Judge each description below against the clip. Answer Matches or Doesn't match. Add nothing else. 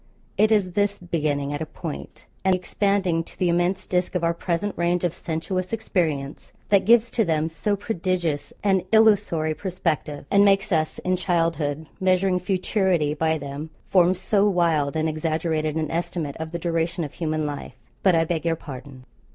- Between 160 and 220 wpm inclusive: Matches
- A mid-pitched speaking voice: Matches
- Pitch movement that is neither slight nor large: Matches